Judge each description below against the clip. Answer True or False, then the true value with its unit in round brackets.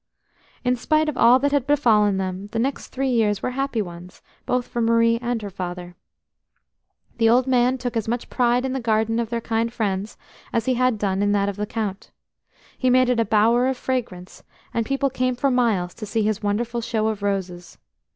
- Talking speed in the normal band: False (210 wpm)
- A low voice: False (230 Hz)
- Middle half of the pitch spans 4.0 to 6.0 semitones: False (3.5 semitones)